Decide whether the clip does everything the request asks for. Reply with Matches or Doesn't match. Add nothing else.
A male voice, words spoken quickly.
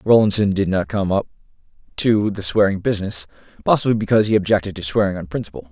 Doesn't match